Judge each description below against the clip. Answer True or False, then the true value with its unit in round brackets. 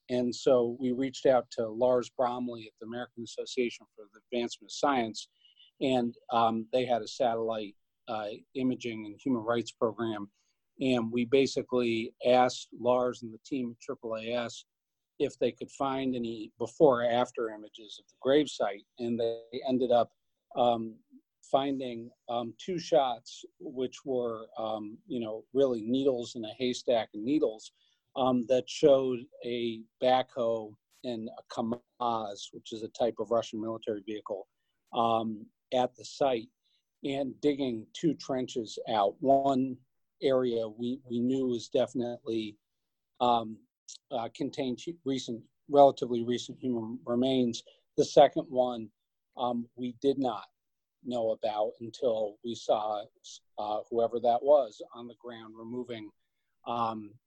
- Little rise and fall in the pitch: True (2.2 semitones)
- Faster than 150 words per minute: False (140 wpm)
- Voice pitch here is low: True (120 Hz)